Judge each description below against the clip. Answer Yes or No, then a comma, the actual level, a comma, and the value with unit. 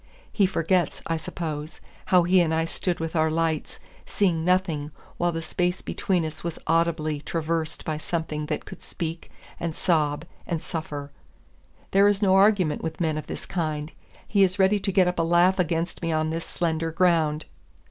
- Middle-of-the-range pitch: Yes, medium, 165 Hz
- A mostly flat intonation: Yes, narrow, 2.3 semitones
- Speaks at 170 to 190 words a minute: Yes, average, 180 wpm